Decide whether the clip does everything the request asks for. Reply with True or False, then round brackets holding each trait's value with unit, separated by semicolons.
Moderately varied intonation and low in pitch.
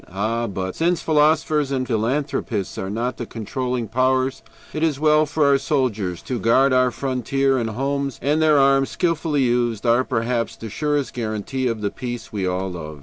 True (3.8 semitones; 130 Hz)